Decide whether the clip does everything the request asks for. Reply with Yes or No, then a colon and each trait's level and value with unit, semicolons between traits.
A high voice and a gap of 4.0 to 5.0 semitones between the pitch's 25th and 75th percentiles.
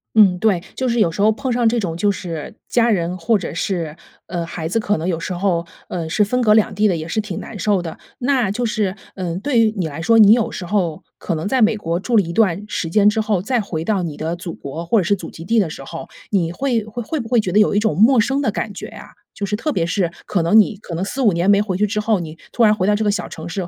Yes: high, 200 Hz; average, 4.4 semitones